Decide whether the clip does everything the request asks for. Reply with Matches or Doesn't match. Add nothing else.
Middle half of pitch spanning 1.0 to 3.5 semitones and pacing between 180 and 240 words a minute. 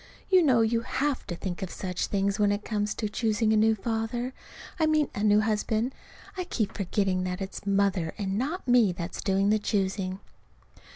Matches